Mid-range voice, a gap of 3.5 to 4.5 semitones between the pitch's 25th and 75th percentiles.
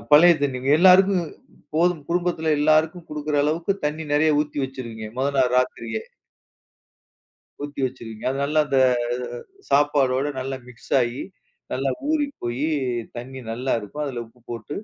Yes: medium, 145 Hz; average, 3.8 semitones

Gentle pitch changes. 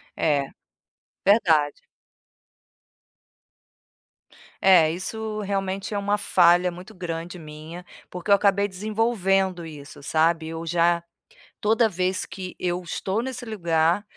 No: average, 3.4 semitones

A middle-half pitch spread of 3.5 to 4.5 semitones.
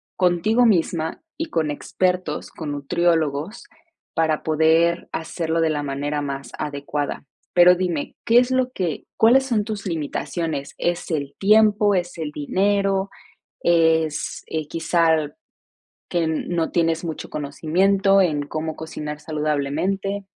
Yes: average, 4.0 semitones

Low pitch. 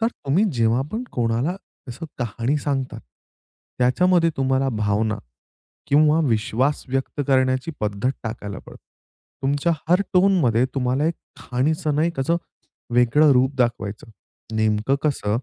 Yes: low, 130 Hz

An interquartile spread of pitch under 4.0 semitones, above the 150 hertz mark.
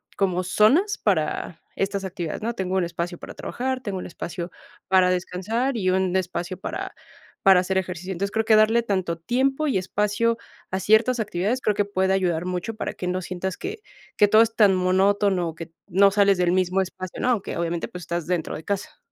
Yes: average, 2.9 semitones; high, 190 Hz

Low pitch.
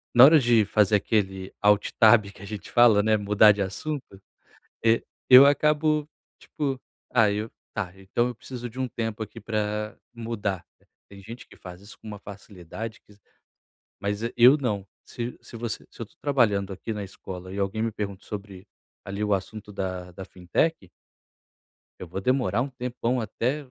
Yes: low, 105 Hz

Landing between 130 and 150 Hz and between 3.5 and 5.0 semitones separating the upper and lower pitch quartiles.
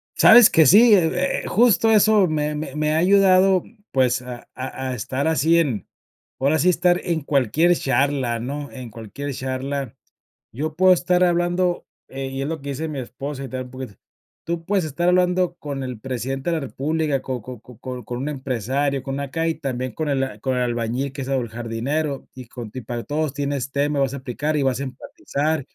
Yes: medium, 140 Hz; average, 3.9 semitones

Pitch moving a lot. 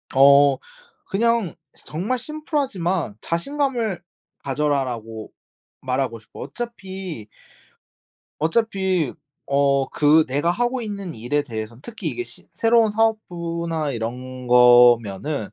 Yes: wide, 9.0 semitones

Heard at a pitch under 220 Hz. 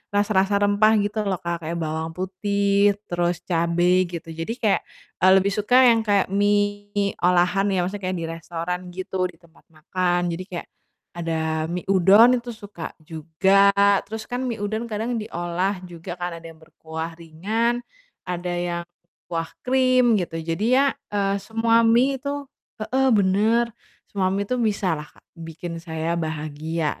Yes: medium, 185 Hz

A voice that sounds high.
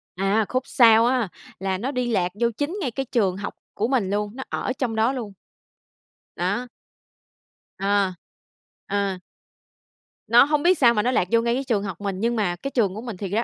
Yes: high, 225 Hz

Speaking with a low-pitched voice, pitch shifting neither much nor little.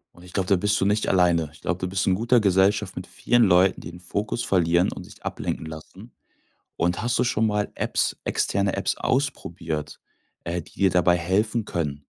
Yes: very low, 95 Hz; average, 3.1 semitones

